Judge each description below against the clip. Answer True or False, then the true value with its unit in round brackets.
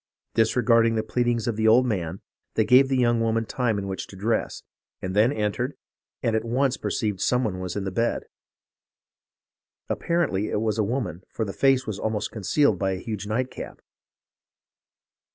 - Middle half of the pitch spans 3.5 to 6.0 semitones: False (3.1 semitones)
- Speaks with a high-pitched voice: False (110 Hz)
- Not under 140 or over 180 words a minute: True (170 wpm)